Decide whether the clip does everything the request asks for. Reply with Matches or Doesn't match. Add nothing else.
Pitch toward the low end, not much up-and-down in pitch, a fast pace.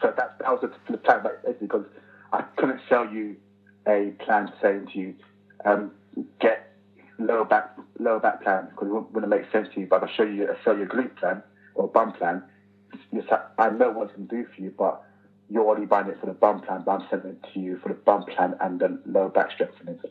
Matches